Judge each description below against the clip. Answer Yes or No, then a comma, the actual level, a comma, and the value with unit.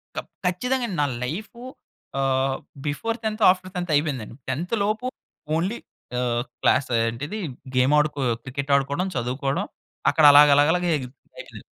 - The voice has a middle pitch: Yes, medium, 145 Hz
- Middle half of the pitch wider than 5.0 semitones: Yes, wide, 5.4 semitones